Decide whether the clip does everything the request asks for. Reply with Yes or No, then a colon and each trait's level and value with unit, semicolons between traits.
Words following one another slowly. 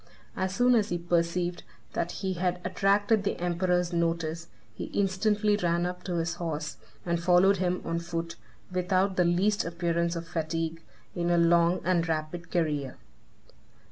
No: average, 155 wpm